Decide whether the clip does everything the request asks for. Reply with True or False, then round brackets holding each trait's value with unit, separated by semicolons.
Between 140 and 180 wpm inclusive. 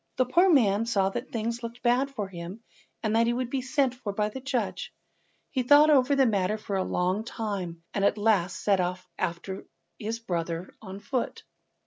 False (195 wpm)